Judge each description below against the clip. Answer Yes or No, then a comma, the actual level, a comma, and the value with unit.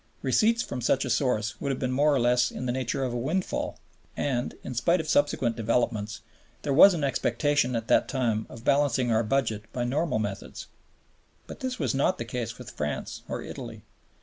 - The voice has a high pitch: No, low, 125 Hz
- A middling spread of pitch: Yes, average, 3.7 semitones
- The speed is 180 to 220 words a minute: Yes, average, 200 wpm